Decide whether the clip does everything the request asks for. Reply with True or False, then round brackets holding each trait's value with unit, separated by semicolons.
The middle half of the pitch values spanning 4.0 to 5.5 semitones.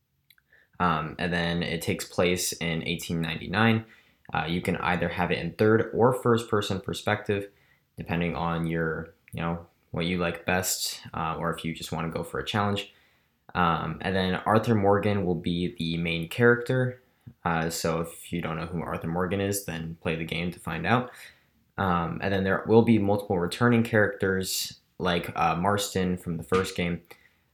False (3.3 semitones)